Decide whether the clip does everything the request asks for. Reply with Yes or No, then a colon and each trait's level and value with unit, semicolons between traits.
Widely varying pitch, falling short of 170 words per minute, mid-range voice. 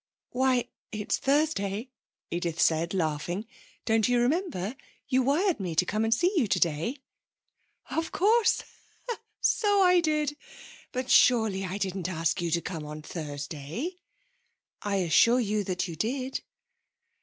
No: wide, 7.8 semitones; average, 140 wpm; high, 215 Hz